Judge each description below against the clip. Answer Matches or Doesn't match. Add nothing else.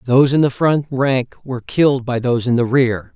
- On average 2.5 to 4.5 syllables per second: Doesn't match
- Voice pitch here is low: Matches